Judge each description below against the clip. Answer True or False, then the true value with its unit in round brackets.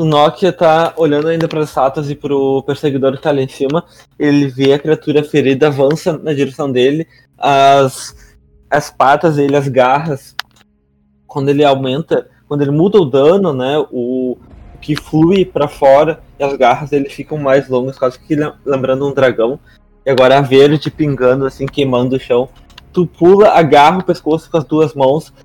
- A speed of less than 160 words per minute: False (175 wpm)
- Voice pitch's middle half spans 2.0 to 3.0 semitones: True (2.5 semitones)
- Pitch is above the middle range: False (140 Hz)